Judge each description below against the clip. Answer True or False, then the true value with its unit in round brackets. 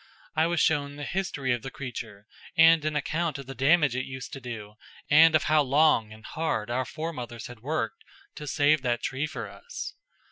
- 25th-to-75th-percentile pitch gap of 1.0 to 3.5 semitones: False (4.3 semitones)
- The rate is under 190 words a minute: False (200 wpm)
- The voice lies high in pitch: False (140 Hz)